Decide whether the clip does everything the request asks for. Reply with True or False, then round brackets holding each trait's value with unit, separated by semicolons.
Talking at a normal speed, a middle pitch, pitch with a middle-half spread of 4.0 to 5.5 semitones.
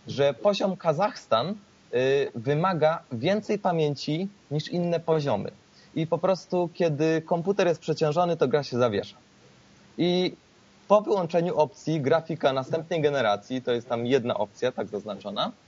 True (135 wpm; 160 Hz; 4.3 semitones)